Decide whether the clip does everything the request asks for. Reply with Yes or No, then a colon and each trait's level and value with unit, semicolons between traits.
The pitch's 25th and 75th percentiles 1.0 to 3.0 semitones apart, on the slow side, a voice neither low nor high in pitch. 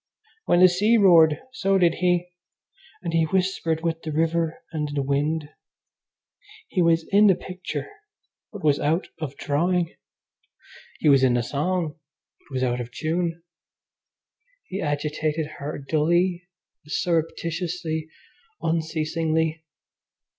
Yes: average, 2.7 semitones; slow, 125 wpm; medium, 160 Hz